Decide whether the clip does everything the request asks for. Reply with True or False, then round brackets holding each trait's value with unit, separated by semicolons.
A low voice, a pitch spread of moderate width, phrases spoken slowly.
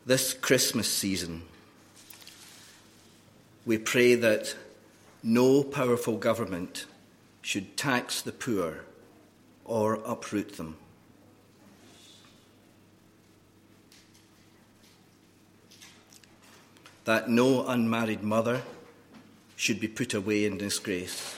False (110 Hz; 1.5 semitones; 75 wpm)